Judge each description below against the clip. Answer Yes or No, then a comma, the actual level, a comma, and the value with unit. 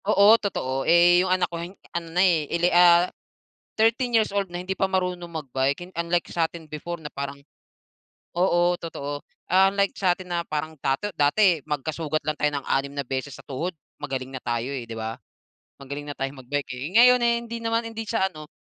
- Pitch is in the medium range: Yes, medium, 170 Hz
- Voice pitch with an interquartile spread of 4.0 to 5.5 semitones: Yes, average, 4.8 semitones